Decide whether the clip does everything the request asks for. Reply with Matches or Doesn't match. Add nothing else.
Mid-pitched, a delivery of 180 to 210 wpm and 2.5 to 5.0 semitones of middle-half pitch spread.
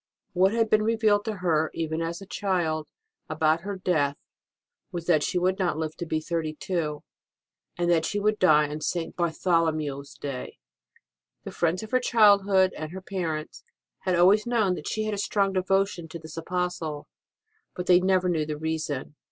Matches